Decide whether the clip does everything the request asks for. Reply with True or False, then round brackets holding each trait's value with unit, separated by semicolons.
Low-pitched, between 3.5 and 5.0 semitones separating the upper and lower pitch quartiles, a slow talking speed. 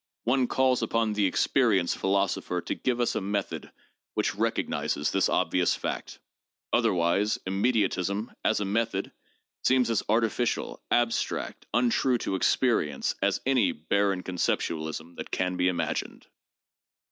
True (100 Hz; 4.4 semitones; 125 wpm)